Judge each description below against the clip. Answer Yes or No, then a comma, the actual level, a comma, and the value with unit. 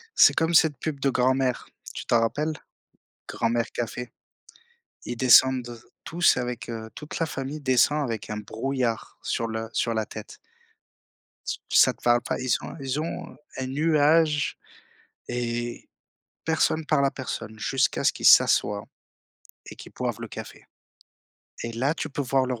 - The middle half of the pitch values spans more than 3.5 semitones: Yes, average, 3.9 semitones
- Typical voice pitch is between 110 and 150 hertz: Yes, low, 130 Hz